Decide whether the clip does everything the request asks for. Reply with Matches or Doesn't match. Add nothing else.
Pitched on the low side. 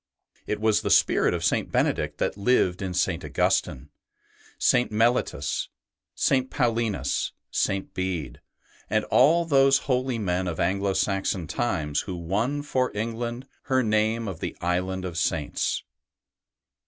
Matches